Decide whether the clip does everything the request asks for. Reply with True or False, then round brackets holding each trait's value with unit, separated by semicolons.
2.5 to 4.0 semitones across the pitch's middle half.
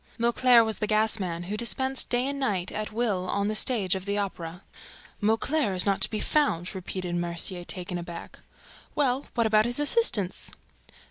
False (4.7 semitones)